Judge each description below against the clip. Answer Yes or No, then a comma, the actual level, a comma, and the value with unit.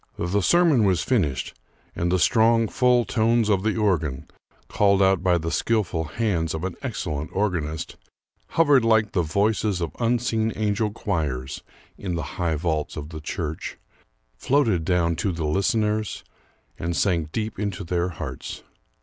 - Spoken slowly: No, average, 150 wpm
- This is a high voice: No, very low, 95 Hz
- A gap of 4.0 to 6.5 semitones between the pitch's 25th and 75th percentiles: Yes, average, 5.0 semitones